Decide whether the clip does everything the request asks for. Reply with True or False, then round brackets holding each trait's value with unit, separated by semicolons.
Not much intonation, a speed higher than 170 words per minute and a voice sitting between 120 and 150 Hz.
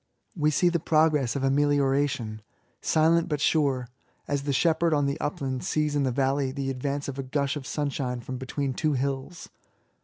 True (2.2 semitones; 180 wpm; 140 Hz)